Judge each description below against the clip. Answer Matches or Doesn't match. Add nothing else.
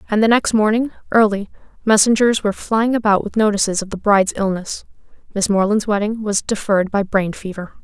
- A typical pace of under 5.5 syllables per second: Doesn't match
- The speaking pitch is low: Doesn't match